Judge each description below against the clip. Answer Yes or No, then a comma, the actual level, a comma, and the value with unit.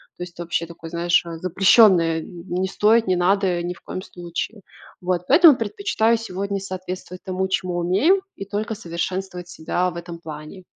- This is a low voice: No, medium, 185 Hz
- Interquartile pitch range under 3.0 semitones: Yes, narrow, 2.4 semitones